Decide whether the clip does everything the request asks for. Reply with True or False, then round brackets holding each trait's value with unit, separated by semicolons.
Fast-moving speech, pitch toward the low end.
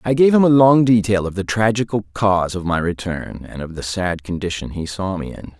True (235 wpm; 100 Hz)